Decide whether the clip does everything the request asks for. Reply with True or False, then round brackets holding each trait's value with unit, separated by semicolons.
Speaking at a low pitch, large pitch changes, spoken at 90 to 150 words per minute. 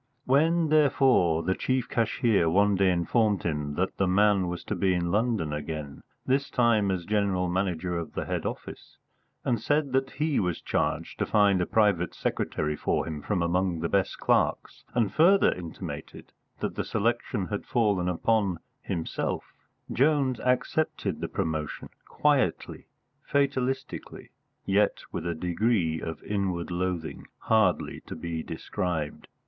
True (95 Hz; 5.8 semitones; 145 wpm)